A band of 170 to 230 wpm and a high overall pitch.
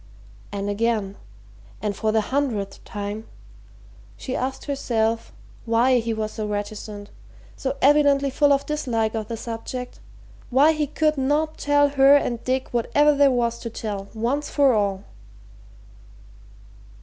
No: slow, 135 wpm; high, 235 Hz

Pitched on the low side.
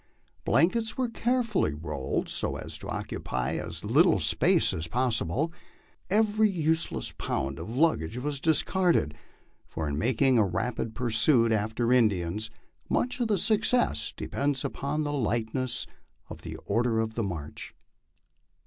Yes: low, 125 Hz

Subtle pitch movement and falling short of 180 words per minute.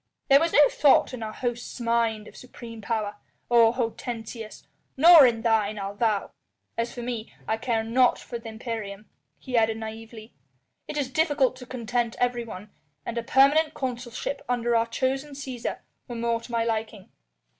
Yes: narrow, 2.2 semitones; average, 165 wpm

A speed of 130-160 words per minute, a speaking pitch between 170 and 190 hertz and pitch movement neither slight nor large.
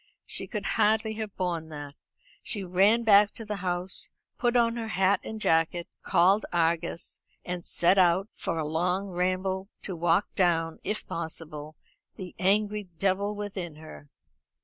Yes: average, 150 wpm; medium, 185 Hz; average, 3.4 semitones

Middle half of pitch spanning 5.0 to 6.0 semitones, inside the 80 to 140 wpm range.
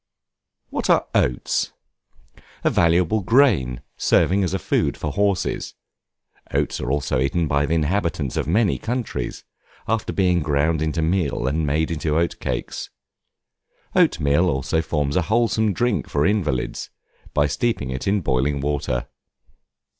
Yes: average, 5.3 semitones; slow, 135 wpm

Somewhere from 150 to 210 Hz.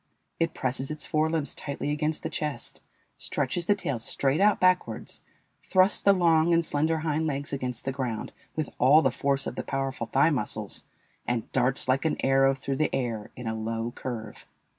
No: medium, 140 Hz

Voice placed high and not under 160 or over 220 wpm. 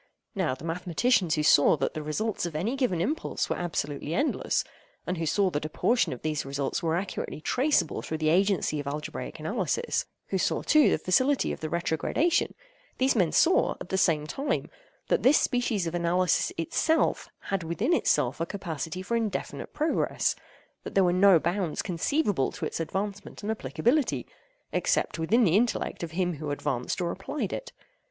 No: medium, 180 Hz; average, 170 wpm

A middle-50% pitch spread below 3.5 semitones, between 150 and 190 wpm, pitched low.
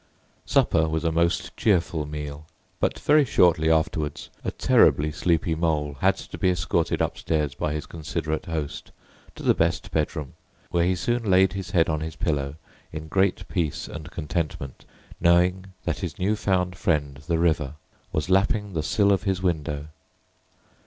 Yes: average, 3.1 semitones; average, 160 wpm; very low, 80 Hz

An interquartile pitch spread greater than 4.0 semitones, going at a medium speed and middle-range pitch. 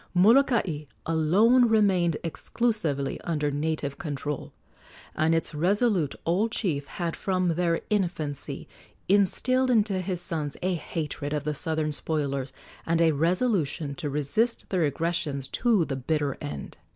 No: average, 4.7 semitones; slow, 130 wpm; medium, 165 Hz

